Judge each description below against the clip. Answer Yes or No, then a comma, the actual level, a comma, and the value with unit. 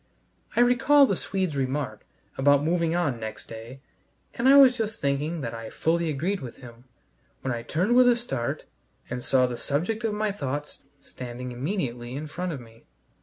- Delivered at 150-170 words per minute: No, average, 180 wpm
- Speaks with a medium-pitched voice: Yes, medium, 145 Hz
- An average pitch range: No, wide, 8.0 semitones